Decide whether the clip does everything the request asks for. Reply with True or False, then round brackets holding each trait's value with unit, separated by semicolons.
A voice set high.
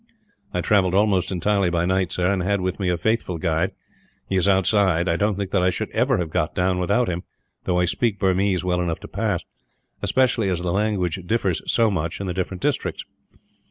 False (95 Hz)